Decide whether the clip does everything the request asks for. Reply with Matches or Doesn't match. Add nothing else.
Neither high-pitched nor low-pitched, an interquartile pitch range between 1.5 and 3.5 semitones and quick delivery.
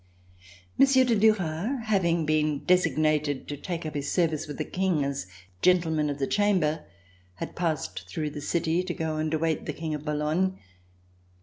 Doesn't match